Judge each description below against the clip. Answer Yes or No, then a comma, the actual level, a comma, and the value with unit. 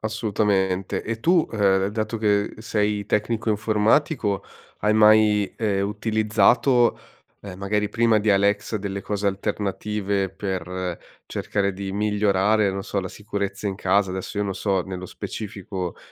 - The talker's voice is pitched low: Yes, low, 105 Hz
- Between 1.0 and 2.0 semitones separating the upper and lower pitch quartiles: Yes, narrow, 1.7 semitones